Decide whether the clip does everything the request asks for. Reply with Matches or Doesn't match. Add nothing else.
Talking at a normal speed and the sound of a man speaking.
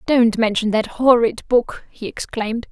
Doesn't match